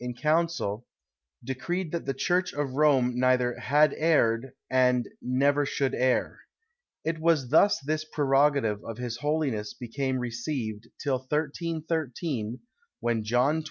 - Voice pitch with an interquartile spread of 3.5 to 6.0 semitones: Yes, average, 3.9 semitones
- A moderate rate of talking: No, slow, 130 wpm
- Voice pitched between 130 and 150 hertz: Yes, low, 135 Hz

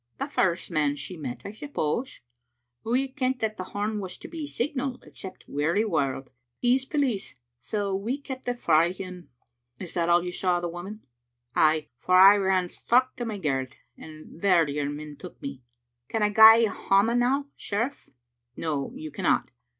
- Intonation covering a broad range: Yes, wide, 7.1 semitones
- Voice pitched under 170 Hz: No, high, 190 Hz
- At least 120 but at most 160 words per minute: No, average, 190 wpm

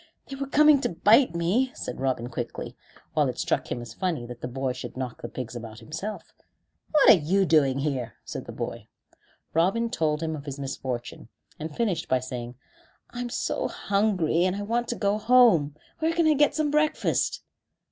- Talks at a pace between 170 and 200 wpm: Yes, average, 190 wpm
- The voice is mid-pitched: Yes, medium, 170 Hz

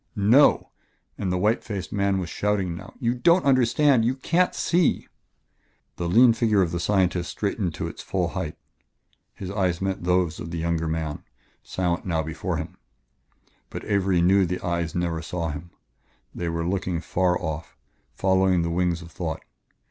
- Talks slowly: No, average, 170 wpm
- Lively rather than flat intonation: No, average, 3.2 semitones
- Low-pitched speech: Yes, very low, 90 Hz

